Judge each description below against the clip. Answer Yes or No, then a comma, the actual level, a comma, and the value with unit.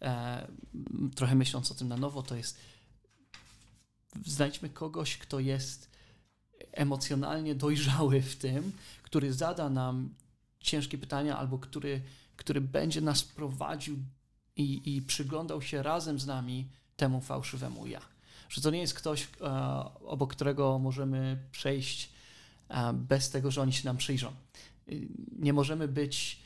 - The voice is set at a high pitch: No, low, 135 Hz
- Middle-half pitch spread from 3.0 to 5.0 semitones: No, narrow, 2.5 semitones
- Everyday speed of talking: Yes, average, 135 wpm